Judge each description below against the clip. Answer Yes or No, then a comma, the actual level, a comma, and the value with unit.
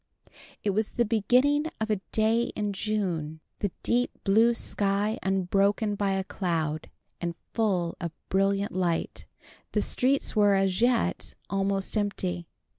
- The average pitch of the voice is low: No, high, 200 Hz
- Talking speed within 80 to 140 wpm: Yes, slow, 135 wpm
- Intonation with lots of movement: No, average, 2.7 semitones